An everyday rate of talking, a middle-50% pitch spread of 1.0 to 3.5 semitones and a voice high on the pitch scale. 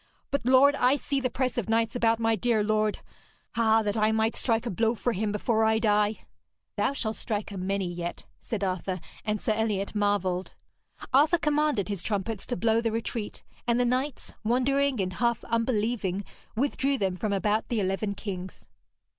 Yes: average, 180 wpm; average, 2.9 semitones; high, 220 Hz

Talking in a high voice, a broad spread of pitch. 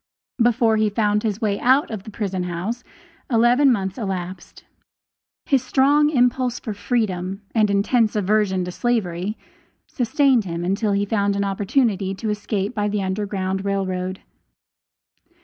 No: high, 210 Hz; average, 3.5 semitones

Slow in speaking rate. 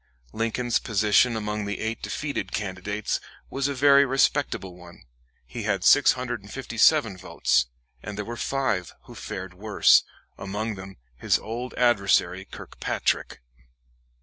Yes: slow, 120 wpm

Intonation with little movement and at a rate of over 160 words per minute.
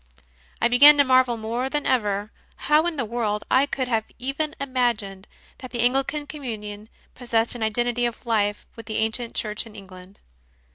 No: average, 3.3 semitones; average, 175 wpm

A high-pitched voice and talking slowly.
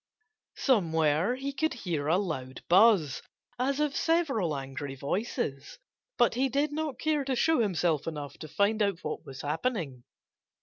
No: high, 200 Hz; average, 155 wpm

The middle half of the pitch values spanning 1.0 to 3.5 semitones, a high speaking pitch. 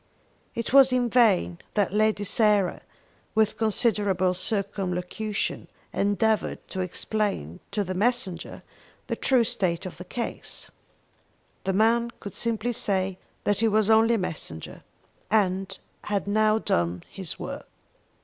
Yes: average, 3.0 semitones; high, 205 Hz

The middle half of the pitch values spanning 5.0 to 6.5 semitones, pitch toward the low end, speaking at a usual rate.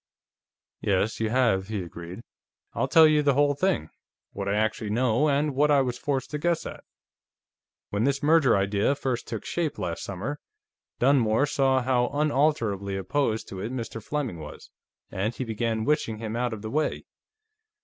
Yes: average, 5.3 semitones; low, 120 Hz; average, 170 wpm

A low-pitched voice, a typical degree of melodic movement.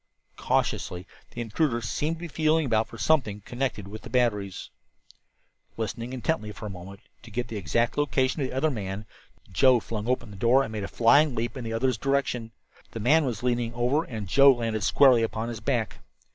Yes: low, 120 Hz; average, 3.5 semitones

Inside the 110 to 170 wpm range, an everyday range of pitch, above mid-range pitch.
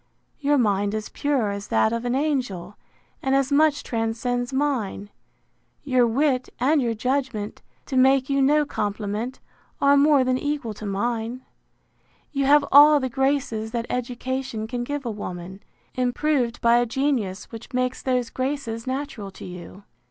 Yes: average, 155 wpm; average, 3.8 semitones; very high, 250 Hz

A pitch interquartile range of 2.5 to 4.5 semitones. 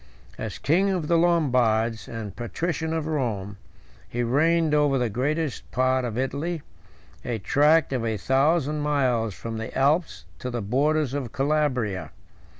No: average, 5.0 semitones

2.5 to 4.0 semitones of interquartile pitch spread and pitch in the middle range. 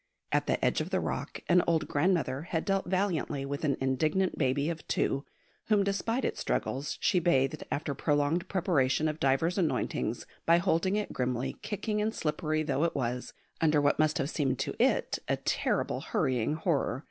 No: average, 4.6 semitones; medium, 155 Hz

